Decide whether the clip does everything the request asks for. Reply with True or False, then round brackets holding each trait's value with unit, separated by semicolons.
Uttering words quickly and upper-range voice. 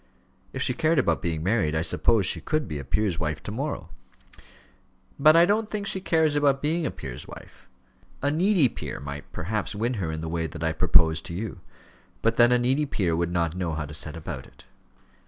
False (215 wpm; 100 Hz)